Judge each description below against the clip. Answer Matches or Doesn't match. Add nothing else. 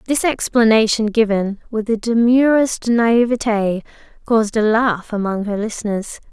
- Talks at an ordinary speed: Doesn't match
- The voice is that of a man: Doesn't match